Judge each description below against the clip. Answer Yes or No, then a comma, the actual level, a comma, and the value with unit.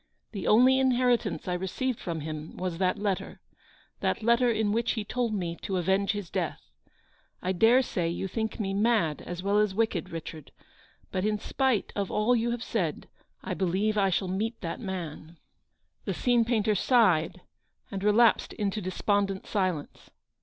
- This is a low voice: No, high, 200 Hz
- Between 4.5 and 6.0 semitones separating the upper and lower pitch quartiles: No, average, 3.7 semitones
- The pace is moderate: Yes, average, 175 wpm